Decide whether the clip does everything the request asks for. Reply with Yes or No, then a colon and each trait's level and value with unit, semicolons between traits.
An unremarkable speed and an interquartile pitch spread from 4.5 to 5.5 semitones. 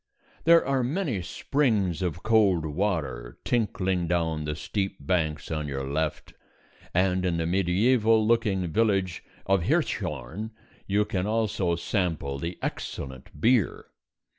No: slow, 125 wpm; average, 5.1 semitones